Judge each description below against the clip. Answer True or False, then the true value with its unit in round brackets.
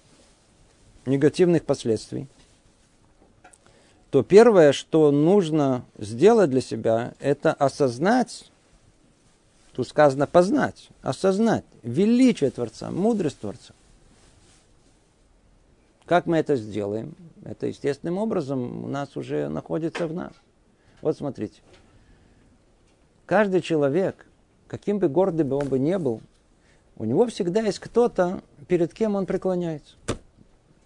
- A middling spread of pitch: False (6.7 semitones)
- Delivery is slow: True (105 wpm)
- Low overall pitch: False (150 Hz)